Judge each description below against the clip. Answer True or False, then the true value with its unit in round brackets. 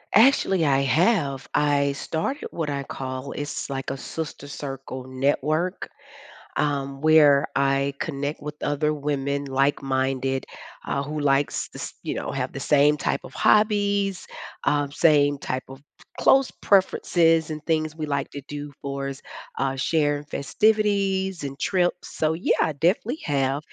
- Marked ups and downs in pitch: False (2.9 semitones)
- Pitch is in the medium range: True (145 Hz)